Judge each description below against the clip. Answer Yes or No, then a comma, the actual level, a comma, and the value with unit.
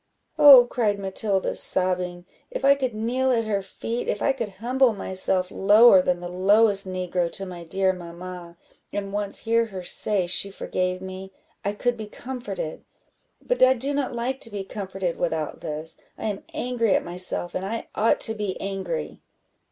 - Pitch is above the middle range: Yes, high, 195 Hz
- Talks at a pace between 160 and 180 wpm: Yes, average, 175 wpm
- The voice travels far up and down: No, average, 4.0 semitones